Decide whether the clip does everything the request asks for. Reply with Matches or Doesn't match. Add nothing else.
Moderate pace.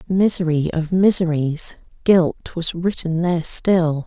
Doesn't match